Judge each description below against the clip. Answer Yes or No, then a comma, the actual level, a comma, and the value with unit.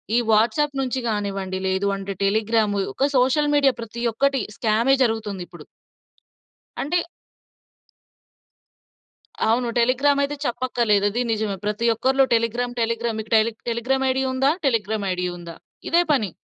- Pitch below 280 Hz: Yes, high, 230 Hz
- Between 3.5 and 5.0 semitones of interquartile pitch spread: Yes, average, 3.8 semitones